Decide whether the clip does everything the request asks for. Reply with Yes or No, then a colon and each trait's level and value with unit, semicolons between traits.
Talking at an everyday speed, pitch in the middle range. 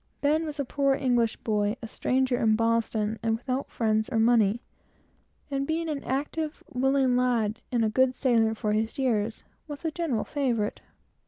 No: average, 170 wpm; high, 245 Hz